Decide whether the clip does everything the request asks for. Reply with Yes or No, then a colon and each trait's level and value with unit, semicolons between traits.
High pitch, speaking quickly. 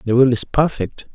No: low, 125 Hz; fast, 210 wpm